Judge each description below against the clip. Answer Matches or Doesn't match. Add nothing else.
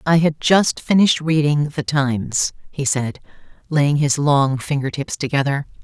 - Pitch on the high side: Doesn't match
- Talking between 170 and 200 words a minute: Doesn't match